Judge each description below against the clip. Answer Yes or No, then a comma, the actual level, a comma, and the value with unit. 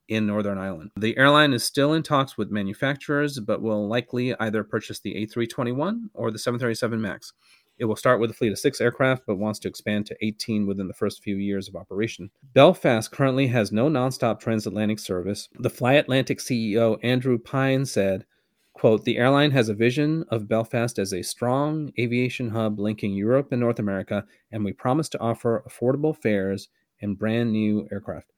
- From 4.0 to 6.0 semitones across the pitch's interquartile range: No, average, 3.6 semitones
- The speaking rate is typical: Yes, average, 185 wpm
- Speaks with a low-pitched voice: Yes, low, 115 Hz